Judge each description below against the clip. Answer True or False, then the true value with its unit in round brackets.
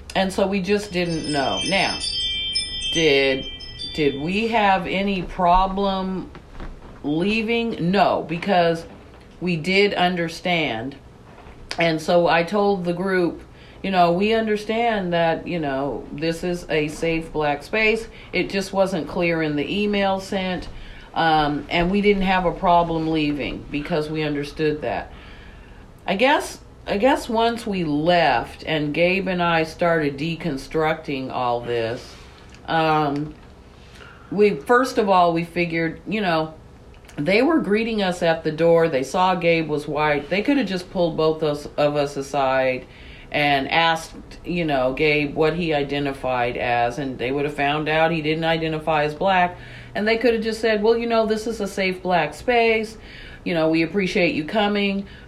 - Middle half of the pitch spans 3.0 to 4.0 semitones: False (4.7 semitones)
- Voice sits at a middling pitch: True (165 Hz)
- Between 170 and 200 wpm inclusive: False (155 wpm)